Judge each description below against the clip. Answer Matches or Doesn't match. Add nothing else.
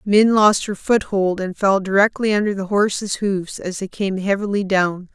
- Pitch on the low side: Doesn't match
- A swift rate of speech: Doesn't match